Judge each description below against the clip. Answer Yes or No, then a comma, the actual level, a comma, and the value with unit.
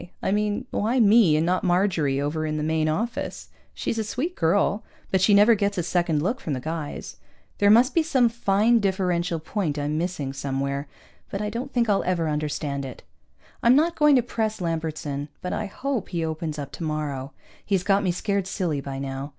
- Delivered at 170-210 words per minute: Yes, average, 200 wpm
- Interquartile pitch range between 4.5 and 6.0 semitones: Yes, wide, 5.6 semitones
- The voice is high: No, medium, 180 Hz